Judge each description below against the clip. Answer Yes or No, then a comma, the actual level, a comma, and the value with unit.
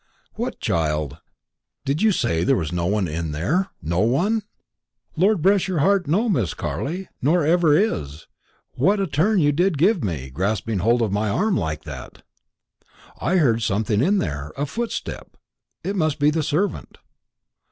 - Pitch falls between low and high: Yes, medium, 145 Hz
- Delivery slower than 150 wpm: No, average, 165 wpm